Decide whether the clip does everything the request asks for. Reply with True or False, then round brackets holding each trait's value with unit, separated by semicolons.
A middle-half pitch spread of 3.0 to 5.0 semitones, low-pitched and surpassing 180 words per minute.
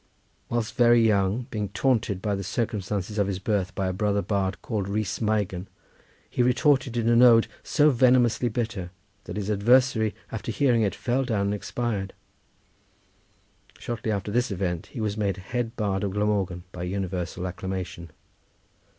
False (3.4 semitones; 105 Hz; 160 wpm)